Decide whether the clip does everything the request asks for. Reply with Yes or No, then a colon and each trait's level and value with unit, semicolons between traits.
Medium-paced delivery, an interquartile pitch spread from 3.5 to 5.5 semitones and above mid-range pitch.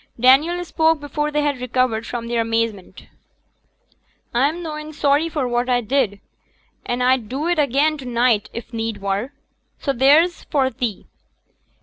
Yes: average, 150 wpm; average, 4.2 semitones; very high, 260 Hz